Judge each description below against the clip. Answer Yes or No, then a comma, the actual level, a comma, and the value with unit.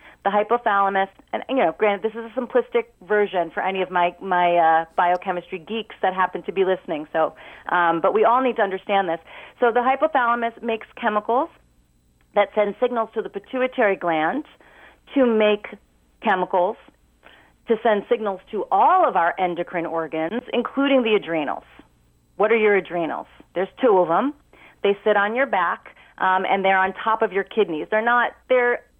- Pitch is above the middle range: Yes, high, 200 Hz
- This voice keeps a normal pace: Yes, average, 175 wpm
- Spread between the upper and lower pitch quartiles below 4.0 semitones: No, average, 4.8 semitones